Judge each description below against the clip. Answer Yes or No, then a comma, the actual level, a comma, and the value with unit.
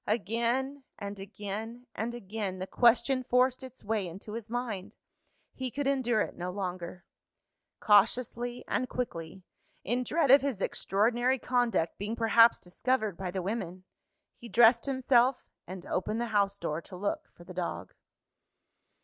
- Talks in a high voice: Yes, high, 225 Hz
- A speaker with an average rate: Yes, average, 150 wpm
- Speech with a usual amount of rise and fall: Yes, average, 4.3 semitones